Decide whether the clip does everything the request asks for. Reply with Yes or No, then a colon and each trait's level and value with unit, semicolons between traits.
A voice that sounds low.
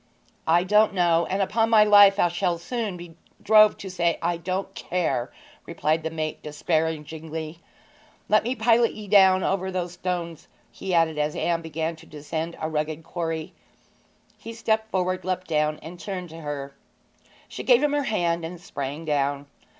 No: medium, 170 Hz